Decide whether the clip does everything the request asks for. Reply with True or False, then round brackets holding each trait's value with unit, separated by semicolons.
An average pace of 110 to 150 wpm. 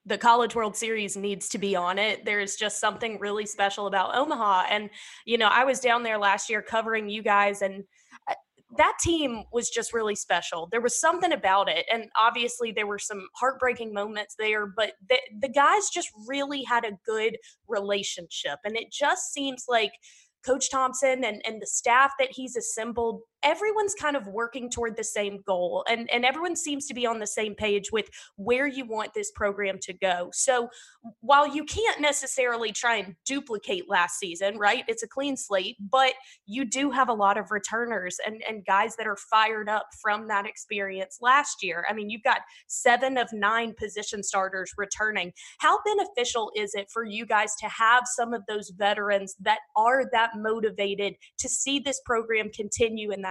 False (190 wpm)